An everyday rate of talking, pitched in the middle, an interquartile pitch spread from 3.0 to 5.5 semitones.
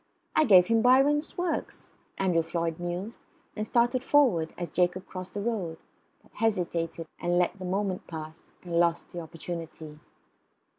Yes: average, 150 wpm; medium, 180 Hz; average, 4.9 semitones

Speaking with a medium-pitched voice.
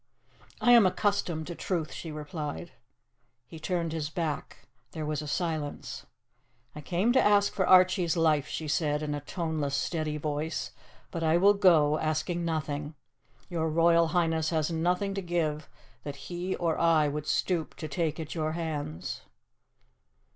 Yes: medium, 160 Hz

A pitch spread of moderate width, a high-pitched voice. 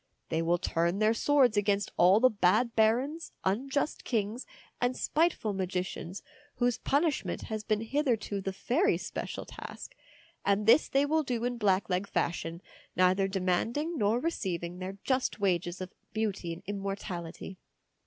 Yes: average, 4.9 semitones; high, 205 Hz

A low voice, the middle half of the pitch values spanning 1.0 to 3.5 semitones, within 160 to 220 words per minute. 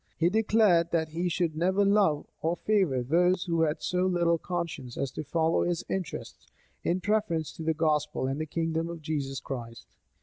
No: medium, 165 Hz; narrow, 2.6 semitones; average, 180 wpm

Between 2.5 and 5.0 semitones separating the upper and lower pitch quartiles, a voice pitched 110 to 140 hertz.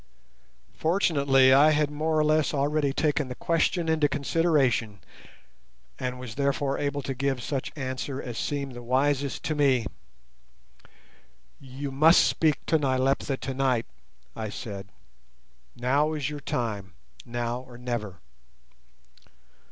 Yes: average, 2.8 semitones; low, 135 Hz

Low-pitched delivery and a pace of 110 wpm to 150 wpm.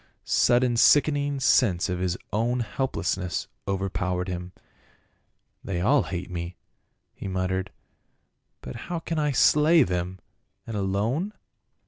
Yes: low, 100 Hz; slow, 135 wpm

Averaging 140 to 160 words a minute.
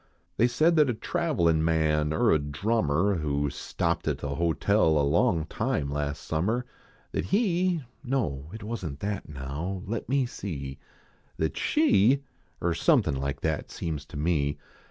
Yes: average, 155 wpm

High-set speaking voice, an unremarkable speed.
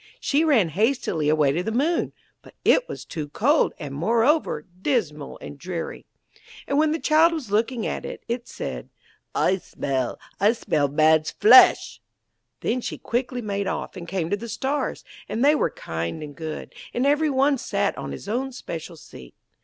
Yes: high, 215 Hz; average, 175 wpm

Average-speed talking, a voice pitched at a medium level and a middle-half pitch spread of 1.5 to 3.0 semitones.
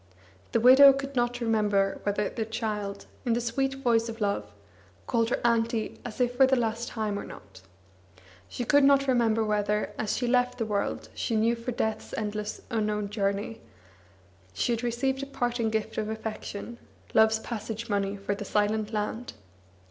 No: average, 170 wpm; high, 225 Hz; narrow, 2.5 semitones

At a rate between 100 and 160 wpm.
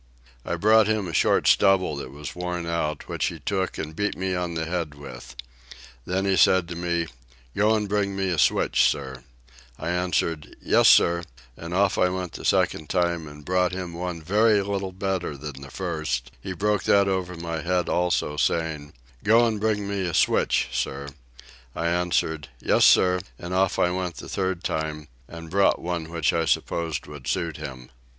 No: average, 185 wpm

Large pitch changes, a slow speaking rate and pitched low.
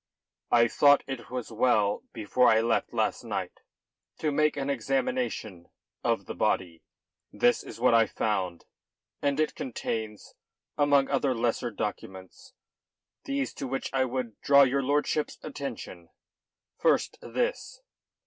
No: average, 4.3 semitones; slow, 130 wpm; low, 130 Hz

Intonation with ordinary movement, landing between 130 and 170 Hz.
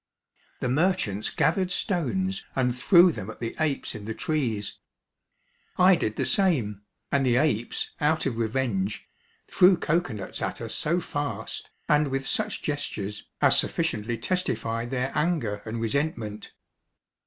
No: wide, 6.9 semitones; low, 135 Hz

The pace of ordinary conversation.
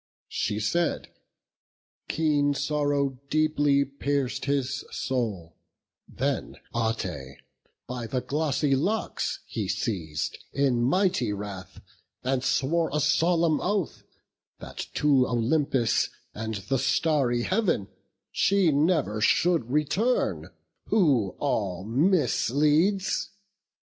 No: slow, 95 wpm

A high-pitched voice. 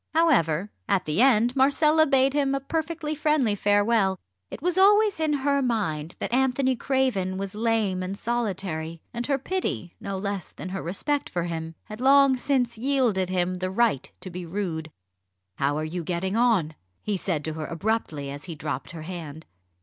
Yes: high, 205 Hz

